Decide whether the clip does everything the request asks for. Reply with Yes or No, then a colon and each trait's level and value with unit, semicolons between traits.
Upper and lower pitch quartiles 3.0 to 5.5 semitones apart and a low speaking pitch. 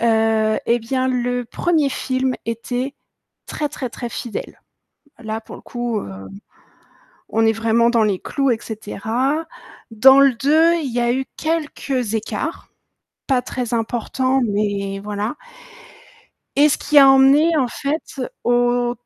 No: average, 3.3 semitones; high, 245 Hz